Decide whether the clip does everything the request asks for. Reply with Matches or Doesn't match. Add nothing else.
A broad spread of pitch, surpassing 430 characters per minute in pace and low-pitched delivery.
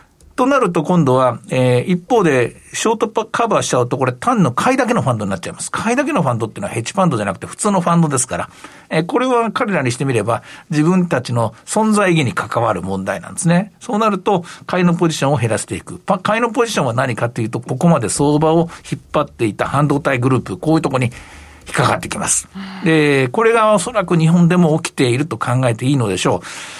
Doesn't match